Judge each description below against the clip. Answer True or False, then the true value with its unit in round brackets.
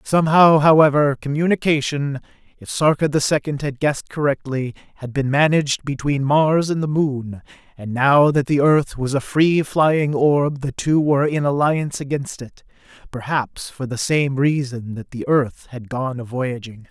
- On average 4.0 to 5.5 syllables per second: True (4.6 syllables/s)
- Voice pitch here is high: False (140 Hz)